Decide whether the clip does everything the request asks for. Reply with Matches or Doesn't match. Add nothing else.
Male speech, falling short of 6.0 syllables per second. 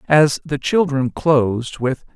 Matches